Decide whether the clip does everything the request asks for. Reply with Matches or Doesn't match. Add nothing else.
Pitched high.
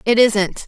Matches